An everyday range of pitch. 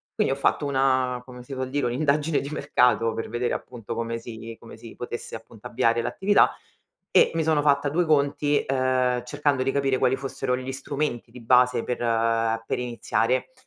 Yes: average, 3.0 semitones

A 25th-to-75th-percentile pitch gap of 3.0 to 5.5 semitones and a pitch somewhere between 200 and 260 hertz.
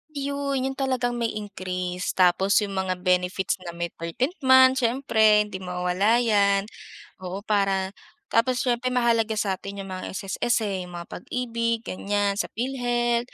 Yes: average, 4.3 semitones; high, 210 Hz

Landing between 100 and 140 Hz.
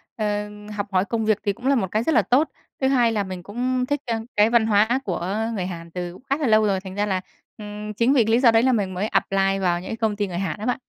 No: high, 210 Hz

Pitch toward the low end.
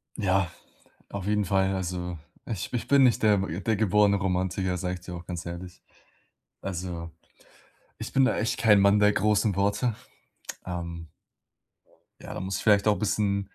Yes: very low, 95 Hz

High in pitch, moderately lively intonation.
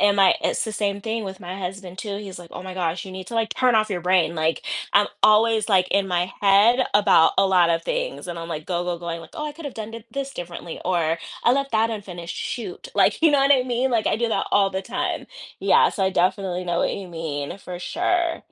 Yes: high, 195 Hz; average, 4.3 semitones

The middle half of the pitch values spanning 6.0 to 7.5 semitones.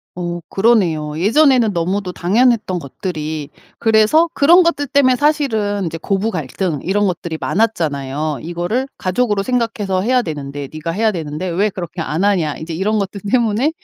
No: wide, 5.6 semitones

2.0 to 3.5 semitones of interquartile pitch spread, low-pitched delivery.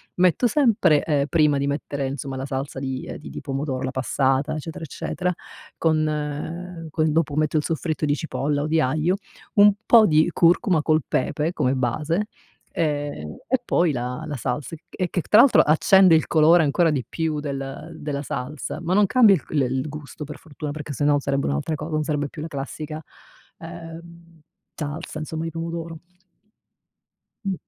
No: average, 2.7 semitones; medium, 155 Hz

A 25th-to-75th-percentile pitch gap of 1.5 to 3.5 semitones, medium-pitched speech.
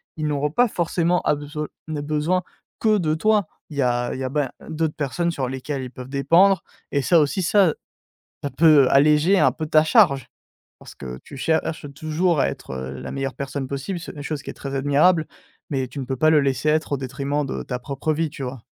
Yes: average, 2.9 semitones; medium, 150 Hz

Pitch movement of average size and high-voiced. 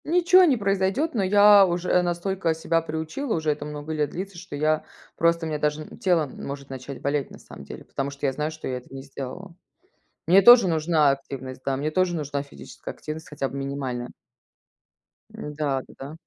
No: average, 4.7 semitones; medium, 155 Hz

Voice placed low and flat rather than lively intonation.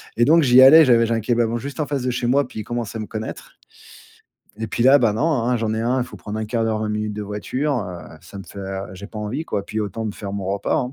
No: low, 115 Hz; average, 3.2 semitones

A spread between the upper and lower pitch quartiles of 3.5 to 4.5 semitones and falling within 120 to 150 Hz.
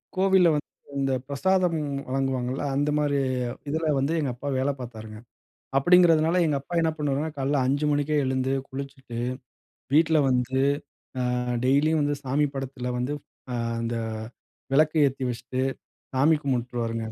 No: average, 3.0 semitones; medium, 140 Hz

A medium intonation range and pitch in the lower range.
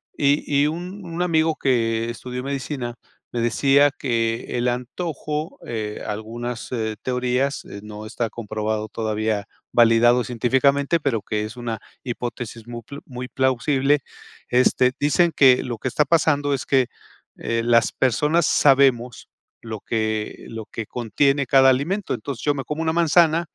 Yes: average, 3.8 semitones; low, 125 Hz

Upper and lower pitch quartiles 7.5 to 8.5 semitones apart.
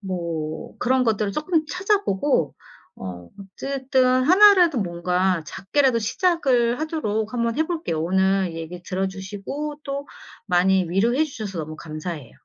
Yes: wide, 7.8 semitones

